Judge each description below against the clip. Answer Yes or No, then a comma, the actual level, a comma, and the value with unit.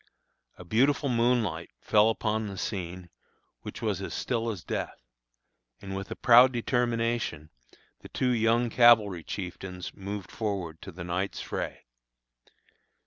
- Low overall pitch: Yes, low, 105 Hz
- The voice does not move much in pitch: No, average, 4.4 semitones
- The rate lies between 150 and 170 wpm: No, slow, 135 wpm